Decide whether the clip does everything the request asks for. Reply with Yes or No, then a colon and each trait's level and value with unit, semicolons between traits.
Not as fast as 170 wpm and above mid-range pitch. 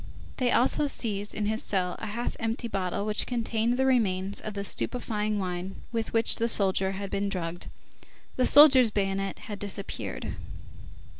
Yes: average, 160 wpm; high, 210 Hz